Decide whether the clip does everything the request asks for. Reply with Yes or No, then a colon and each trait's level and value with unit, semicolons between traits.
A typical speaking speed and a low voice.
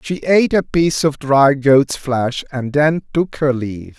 No: average, 195 wpm; medium, 145 Hz